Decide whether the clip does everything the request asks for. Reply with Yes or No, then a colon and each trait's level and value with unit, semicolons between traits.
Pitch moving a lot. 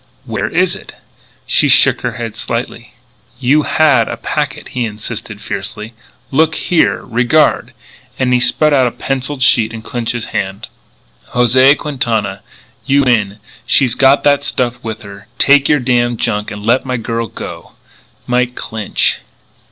No: average, 3.4 semitones